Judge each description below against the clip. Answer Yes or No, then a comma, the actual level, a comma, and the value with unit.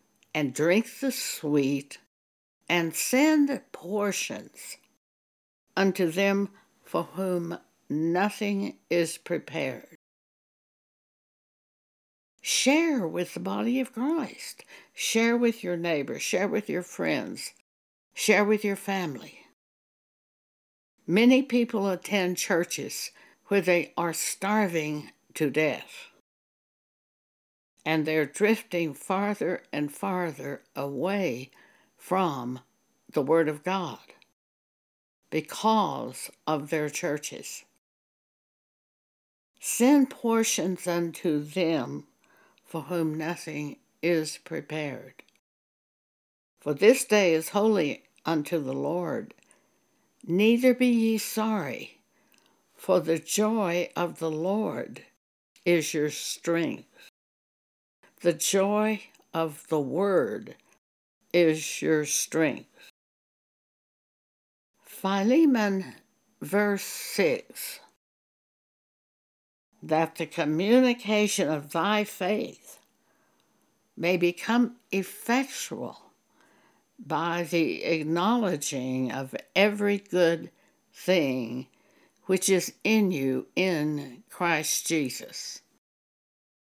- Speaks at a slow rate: Yes, slow, 85 wpm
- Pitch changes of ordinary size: Yes, average, 5.0 semitones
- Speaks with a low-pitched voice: No, medium, 175 Hz